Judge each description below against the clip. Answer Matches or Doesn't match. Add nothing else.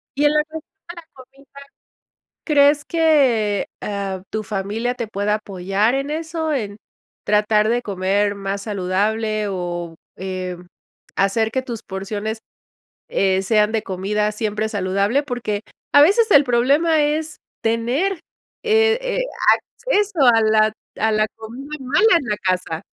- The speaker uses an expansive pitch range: Matches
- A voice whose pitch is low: Doesn't match